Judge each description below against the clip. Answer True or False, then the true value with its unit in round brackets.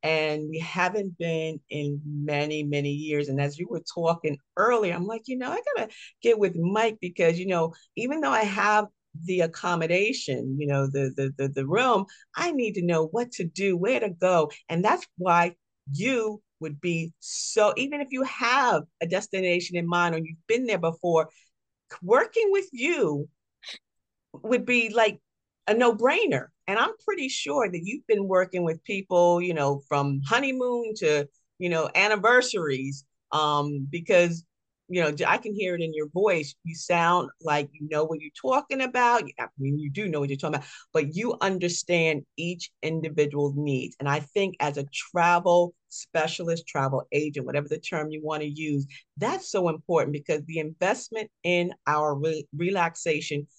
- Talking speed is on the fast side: False (175 wpm)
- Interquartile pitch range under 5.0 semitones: False (5.5 semitones)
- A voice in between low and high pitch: True (170 Hz)